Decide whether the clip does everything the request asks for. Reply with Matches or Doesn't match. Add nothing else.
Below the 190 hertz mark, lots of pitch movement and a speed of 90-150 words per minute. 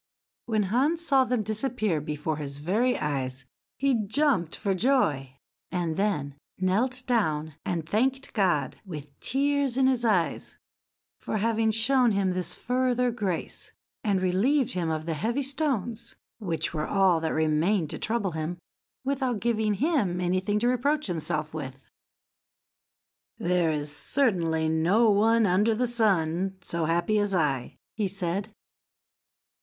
Doesn't match